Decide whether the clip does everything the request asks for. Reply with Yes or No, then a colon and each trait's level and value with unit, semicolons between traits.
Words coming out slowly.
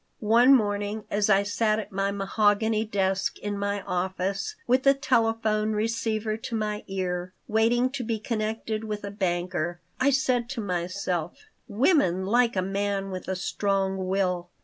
No: average, 155 wpm